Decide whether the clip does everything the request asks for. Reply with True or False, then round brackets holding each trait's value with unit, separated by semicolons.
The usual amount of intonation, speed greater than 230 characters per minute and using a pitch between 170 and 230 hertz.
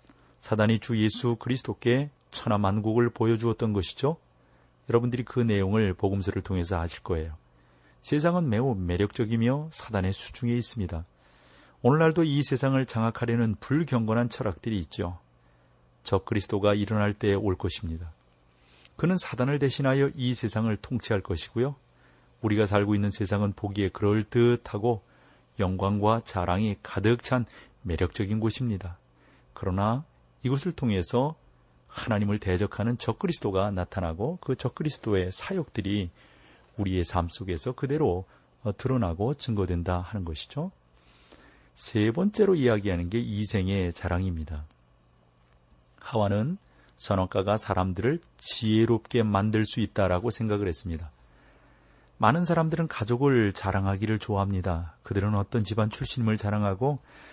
False (4.7 semitones; 315 characters per minute; 105 Hz)